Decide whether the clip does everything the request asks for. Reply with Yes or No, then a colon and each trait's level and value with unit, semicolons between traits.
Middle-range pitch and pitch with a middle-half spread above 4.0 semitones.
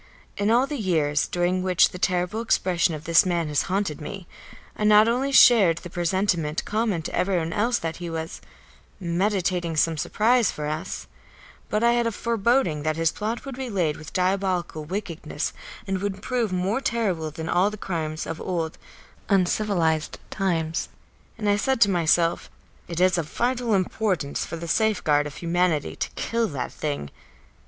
Yes: medium, 180 Hz; average, 4.4 semitones